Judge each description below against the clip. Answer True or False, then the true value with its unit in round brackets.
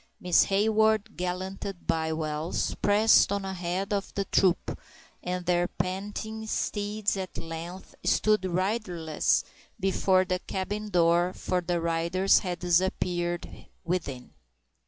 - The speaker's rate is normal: False (115 wpm)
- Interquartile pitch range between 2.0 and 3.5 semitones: True (2.4 semitones)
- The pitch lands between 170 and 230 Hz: True (185 Hz)